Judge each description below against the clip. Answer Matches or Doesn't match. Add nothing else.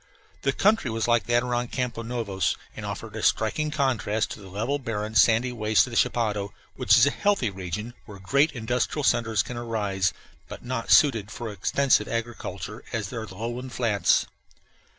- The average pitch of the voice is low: Matches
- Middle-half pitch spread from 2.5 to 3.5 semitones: Matches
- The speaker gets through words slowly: Doesn't match